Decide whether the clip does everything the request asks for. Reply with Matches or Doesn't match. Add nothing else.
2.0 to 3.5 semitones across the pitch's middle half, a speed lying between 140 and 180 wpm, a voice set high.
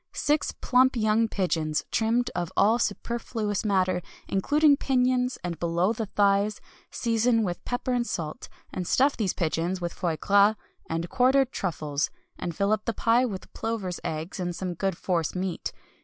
Doesn't match